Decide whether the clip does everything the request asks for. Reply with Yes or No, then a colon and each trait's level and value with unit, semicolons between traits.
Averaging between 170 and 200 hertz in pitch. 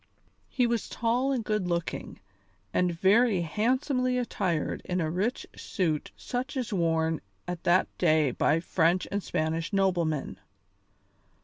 Yes: medium, 185 Hz